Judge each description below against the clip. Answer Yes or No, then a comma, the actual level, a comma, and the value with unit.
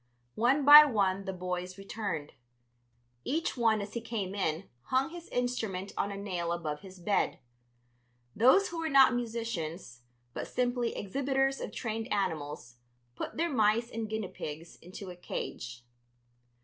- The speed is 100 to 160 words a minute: Yes, average, 150 wpm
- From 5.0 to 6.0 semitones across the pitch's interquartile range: Yes, wide, 5.4 semitones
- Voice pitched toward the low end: No, high, 205 Hz